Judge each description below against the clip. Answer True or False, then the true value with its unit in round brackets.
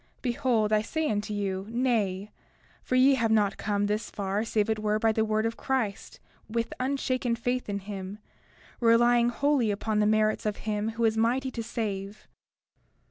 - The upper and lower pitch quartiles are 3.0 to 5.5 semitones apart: False (2.4 semitones)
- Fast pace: False (175 wpm)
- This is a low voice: False (220 Hz)